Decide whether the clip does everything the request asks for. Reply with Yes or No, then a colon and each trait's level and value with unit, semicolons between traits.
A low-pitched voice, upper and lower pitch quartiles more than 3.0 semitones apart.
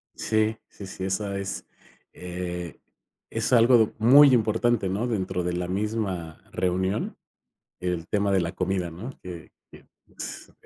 Yes: very low, 95 Hz; average, 3.5 semitones